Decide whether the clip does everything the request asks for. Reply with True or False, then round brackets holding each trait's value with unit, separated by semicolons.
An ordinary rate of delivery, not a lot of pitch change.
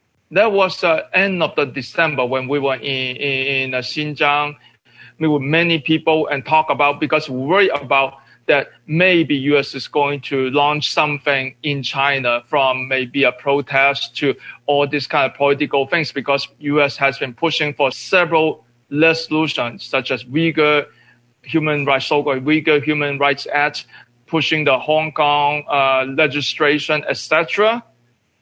True (155 wpm; 2.3 semitones)